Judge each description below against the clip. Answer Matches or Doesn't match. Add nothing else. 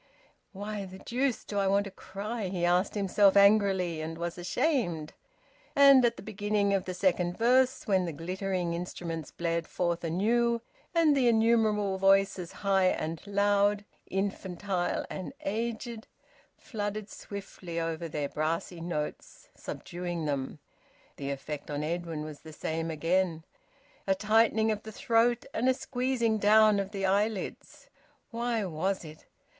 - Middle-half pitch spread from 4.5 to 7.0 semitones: Doesn't match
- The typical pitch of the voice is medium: Doesn't match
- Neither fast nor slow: Matches